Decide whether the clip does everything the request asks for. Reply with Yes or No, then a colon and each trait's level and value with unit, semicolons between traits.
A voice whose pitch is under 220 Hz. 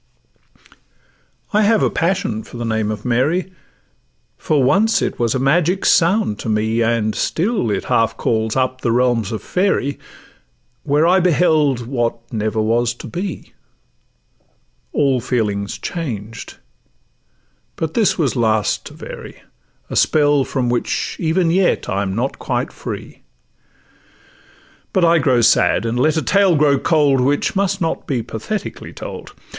Yes: low, 135 Hz